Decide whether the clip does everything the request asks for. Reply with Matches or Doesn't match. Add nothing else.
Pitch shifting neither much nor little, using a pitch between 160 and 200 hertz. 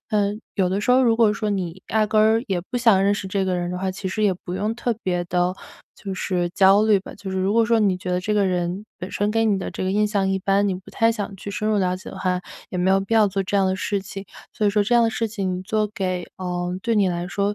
Doesn't match